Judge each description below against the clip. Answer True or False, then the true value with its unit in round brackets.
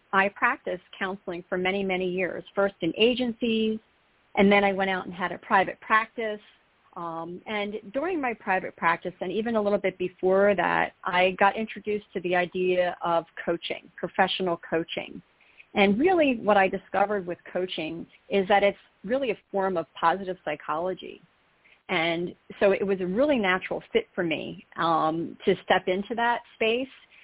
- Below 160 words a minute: False (165 wpm)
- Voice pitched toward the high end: True (195 Hz)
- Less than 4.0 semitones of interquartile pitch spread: True (2.9 semitones)